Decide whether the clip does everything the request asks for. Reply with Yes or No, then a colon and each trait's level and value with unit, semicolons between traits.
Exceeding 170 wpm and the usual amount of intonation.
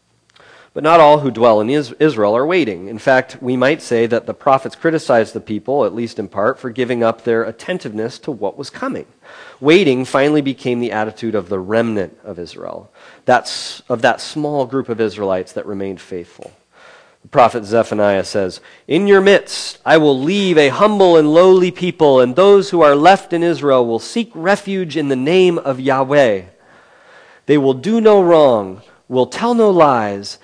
No: average, 180 wpm; wide, 6.4 semitones